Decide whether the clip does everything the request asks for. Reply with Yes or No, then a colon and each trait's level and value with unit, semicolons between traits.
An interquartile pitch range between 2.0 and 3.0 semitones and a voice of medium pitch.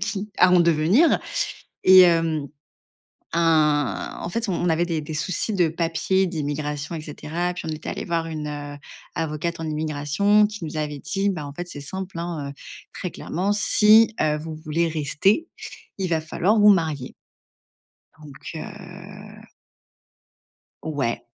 No: average, 3.6 semitones; medium, 165 Hz